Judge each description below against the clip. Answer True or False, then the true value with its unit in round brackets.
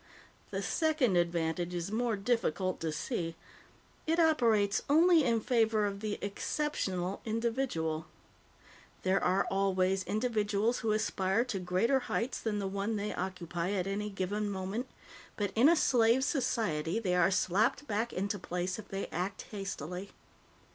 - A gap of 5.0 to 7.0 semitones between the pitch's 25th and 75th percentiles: False (3.8 semitones)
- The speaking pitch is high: True (205 Hz)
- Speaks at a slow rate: False (145 wpm)